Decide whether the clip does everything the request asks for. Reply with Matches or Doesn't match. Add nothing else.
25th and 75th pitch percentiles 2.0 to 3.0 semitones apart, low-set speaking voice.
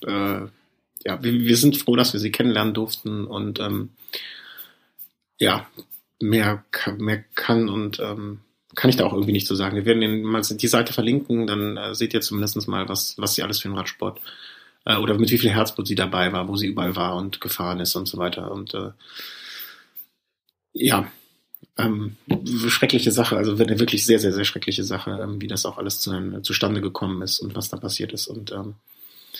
Matches